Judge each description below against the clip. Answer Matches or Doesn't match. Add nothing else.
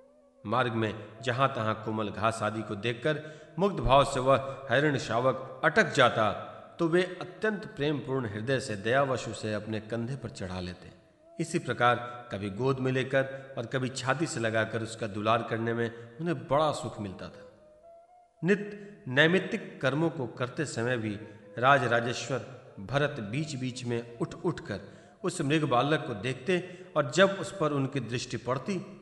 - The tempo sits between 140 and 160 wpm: Matches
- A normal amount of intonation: Doesn't match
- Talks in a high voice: Doesn't match